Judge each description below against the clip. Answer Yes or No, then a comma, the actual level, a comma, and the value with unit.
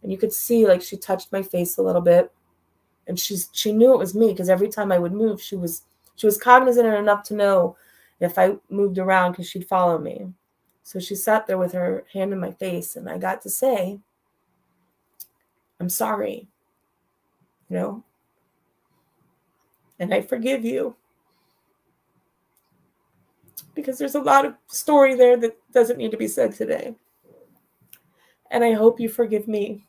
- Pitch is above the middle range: Yes, high, 205 Hz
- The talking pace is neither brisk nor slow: Yes, average, 170 wpm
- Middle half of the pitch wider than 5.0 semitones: No, average, 4.2 semitones